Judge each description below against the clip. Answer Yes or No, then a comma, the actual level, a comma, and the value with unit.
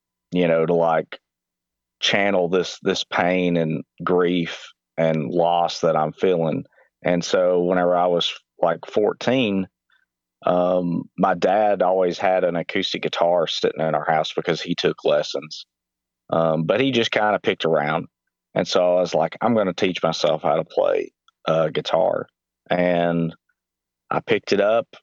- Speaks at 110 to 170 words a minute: Yes, average, 160 wpm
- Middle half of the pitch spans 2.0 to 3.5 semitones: Yes, narrow, 2.4 semitones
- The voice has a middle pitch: No, very low, 85 Hz